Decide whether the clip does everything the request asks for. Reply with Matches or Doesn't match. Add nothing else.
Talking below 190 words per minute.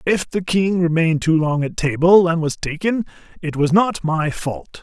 Doesn't match